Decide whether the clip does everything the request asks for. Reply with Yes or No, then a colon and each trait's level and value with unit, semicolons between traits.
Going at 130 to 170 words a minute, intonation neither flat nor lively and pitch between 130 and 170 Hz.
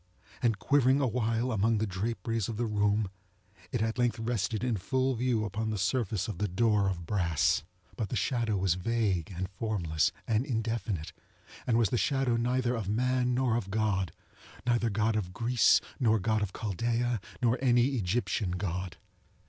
No: average, 165 wpm; average, 3.5 semitones; low, 110 Hz